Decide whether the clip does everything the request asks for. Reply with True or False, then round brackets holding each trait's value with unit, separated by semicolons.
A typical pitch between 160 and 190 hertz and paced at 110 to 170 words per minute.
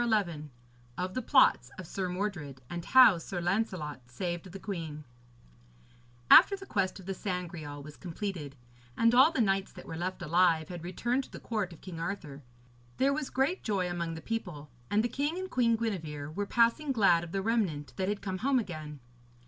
False (185 Hz; 190 wpm)